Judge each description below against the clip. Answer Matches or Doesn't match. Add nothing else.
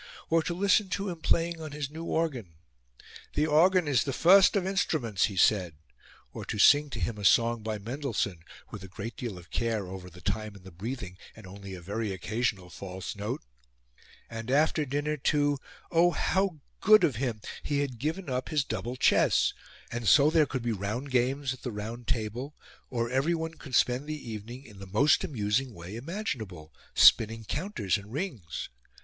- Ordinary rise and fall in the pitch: Doesn't match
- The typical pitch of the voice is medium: Doesn't match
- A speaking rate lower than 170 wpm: Doesn't match